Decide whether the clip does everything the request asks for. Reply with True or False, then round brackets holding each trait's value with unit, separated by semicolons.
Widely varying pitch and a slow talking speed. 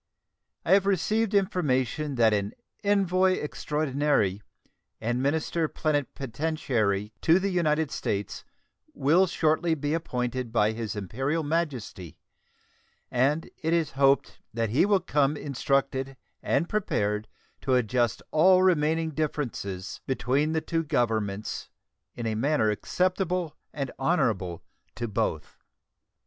True (6.0 semitones; 115 wpm)